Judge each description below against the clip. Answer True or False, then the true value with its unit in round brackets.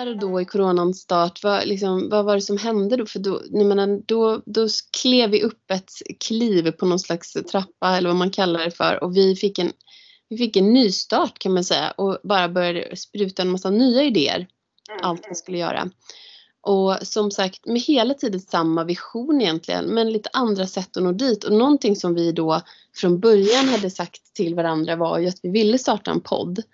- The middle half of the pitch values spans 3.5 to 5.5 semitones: True (3.8 semitones)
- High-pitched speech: True (195 Hz)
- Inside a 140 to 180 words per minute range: False (195 wpm)